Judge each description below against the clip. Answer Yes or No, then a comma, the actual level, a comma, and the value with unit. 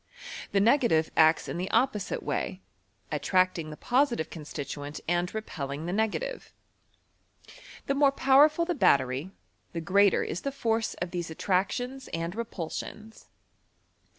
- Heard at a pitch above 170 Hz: Yes, high, 190 Hz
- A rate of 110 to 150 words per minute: Yes, average, 140 wpm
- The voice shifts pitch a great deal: Yes, wide, 7.3 semitones